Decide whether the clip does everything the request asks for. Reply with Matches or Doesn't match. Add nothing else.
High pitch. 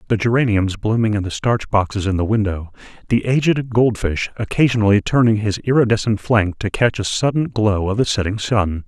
Doesn't match